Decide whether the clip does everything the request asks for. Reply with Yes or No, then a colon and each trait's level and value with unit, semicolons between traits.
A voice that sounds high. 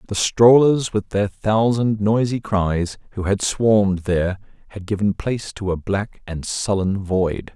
No: low, 100 Hz